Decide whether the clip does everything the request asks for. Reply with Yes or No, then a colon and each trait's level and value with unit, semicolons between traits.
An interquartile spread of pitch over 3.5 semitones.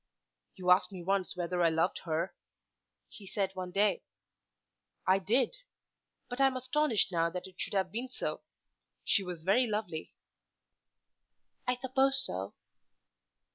Yes: wide, 5.5 semitones